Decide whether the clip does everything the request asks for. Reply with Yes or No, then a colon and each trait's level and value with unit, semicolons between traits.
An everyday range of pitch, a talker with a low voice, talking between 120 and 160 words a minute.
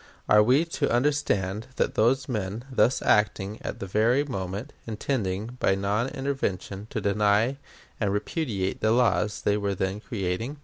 Yes: average, 4.1 semitones; low, 105 Hz; average, 150 wpm